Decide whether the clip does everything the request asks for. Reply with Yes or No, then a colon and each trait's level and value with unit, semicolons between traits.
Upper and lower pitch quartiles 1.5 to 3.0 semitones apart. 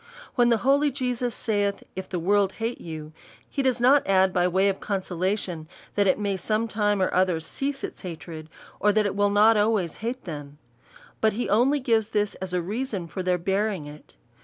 No: average, 3.7 semitones